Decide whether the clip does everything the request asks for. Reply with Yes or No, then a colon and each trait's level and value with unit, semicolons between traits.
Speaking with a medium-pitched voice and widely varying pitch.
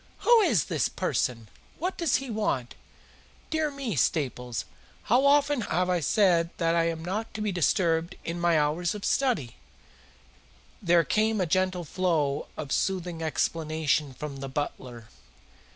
Yes: medium, 170 Hz; wide, 6.0 semitones